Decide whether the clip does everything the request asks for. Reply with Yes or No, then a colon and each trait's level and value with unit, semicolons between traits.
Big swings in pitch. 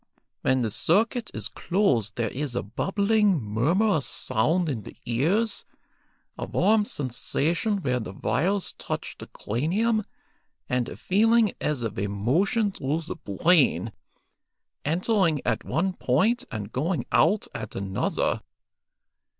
Yes: wide, 9.0 semitones